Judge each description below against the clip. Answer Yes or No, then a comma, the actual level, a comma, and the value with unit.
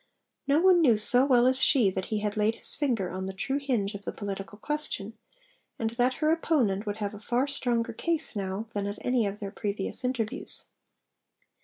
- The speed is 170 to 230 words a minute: Yes, average, 200 wpm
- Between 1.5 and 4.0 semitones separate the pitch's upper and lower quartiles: No, average, 4.4 semitones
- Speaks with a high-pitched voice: Yes, high, 225 Hz